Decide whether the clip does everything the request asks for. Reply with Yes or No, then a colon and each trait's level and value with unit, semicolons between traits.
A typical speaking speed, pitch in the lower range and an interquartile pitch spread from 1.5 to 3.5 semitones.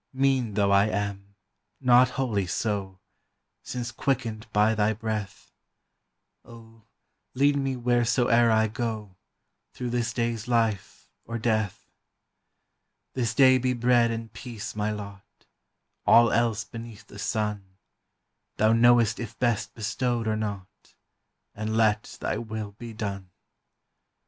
No: slow, 125 wpm; low, 110 Hz; narrow, 2.4 semitones